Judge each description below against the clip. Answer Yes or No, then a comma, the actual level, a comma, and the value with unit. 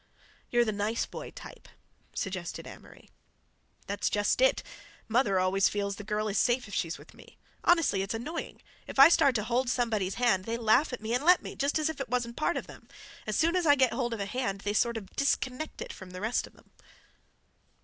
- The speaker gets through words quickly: Yes, fast, 220 wpm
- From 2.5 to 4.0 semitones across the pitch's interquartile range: No, average, 4.5 semitones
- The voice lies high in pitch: Yes, high, 235 Hz